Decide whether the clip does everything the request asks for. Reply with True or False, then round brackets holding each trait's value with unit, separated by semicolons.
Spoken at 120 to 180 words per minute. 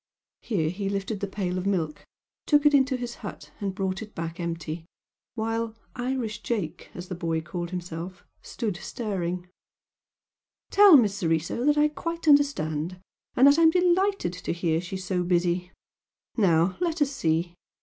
True (165 wpm)